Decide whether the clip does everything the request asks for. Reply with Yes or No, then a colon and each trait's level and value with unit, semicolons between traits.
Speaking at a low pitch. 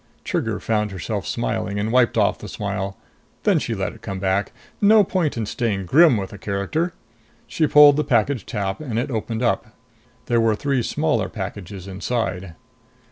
Yes: low, 110 Hz